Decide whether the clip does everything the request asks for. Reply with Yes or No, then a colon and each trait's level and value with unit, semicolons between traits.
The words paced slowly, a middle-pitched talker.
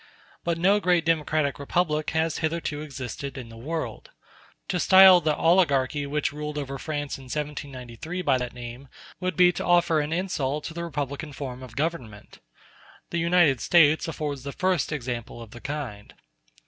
No: average, 165 wpm; medium, 150 Hz